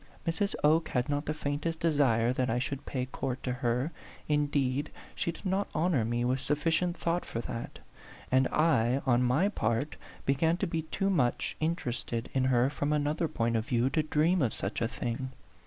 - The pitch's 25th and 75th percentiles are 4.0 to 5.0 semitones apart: Yes, average, 4.5 semitones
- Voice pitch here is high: No, medium, 140 Hz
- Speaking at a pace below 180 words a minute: No, average, 190 wpm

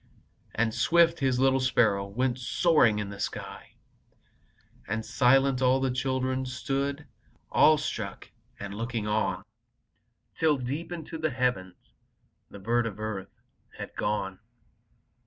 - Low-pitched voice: Yes, low, 125 Hz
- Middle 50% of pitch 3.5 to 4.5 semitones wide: Yes, average, 3.9 semitones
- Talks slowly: Yes, slow, 120 wpm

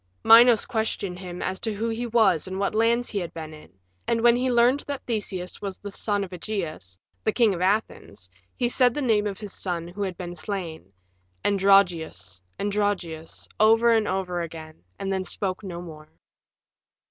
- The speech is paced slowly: No, average, 180 wpm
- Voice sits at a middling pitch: No, high, 195 Hz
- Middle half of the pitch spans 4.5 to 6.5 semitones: No, average, 4.1 semitones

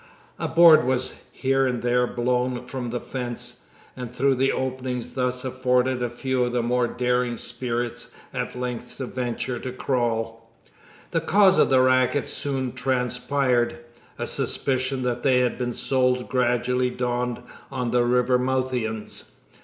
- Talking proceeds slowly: No, average, 145 wpm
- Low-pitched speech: Yes, low, 125 Hz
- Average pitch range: No, narrow, 1.1 semitones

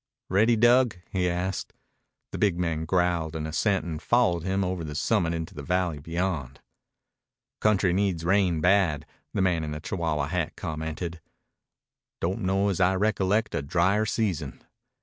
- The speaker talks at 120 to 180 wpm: Yes, average, 160 wpm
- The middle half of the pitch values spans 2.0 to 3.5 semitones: Yes, average, 3.2 semitones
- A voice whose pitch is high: No, very low, 90 Hz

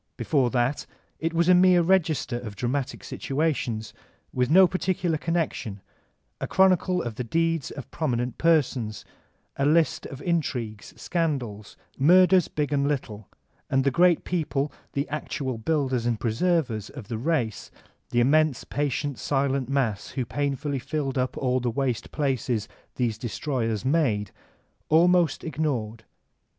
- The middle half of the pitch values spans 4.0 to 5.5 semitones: Yes, average, 5.1 semitones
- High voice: No, medium, 140 Hz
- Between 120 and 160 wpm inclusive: Yes, average, 140 wpm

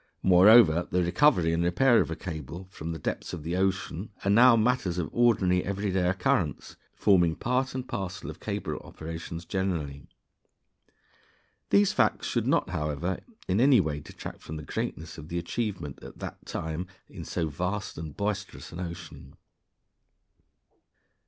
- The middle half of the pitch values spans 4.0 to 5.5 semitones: No, average, 3.6 semitones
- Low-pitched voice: Yes, very low, 90 Hz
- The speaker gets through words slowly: No, average, 160 wpm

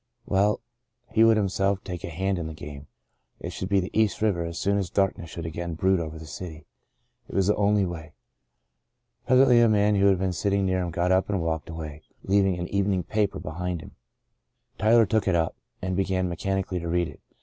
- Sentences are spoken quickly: Yes, fast, 210 wpm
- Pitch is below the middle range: Yes, very low, 95 Hz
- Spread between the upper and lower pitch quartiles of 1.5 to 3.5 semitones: Yes, average, 2.9 semitones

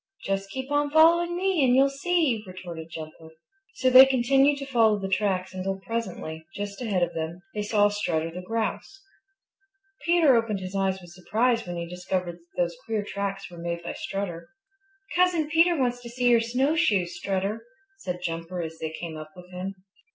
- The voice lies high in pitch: Yes, high, 200 Hz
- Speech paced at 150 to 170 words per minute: No, average, 180 wpm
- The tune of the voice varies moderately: No, wide, 6.5 semitones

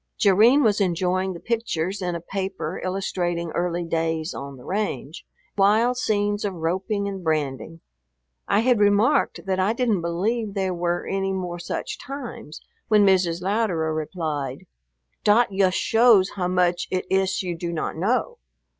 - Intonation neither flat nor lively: Yes, average, 3.2 semitones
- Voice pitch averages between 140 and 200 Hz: Yes, medium, 185 Hz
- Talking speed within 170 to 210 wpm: No, average, 155 wpm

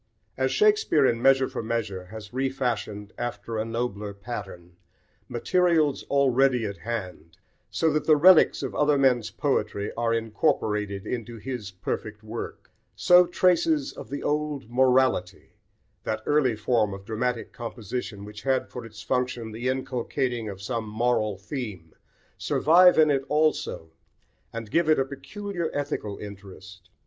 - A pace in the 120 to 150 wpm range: Yes, average, 140 wpm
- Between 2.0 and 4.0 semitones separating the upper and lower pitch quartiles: No, average, 4.7 semitones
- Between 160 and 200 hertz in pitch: No, low, 120 Hz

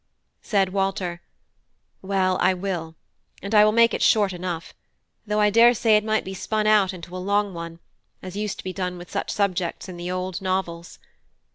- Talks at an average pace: Yes, average, 185 wpm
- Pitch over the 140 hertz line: Yes, high, 190 Hz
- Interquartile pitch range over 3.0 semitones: No, narrow, 2.6 semitones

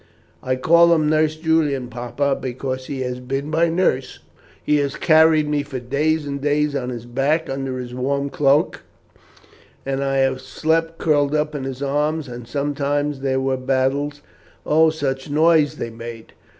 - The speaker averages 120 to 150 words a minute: No, average, 170 wpm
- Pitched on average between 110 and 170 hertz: Yes, medium, 140 Hz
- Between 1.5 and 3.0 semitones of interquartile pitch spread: Yes, narrow, 2.5 semitones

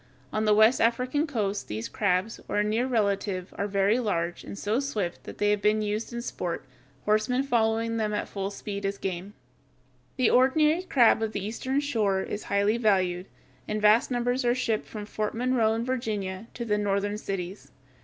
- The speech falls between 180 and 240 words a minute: Yes, average, 185 wpm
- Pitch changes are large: No, average, 3.0 semitones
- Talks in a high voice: Yes, high, 215 Hz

